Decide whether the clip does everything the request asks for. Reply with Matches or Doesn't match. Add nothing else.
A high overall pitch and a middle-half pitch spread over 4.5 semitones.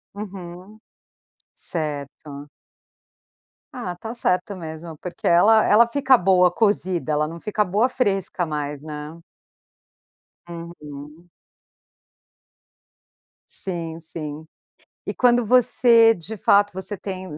Doesn't match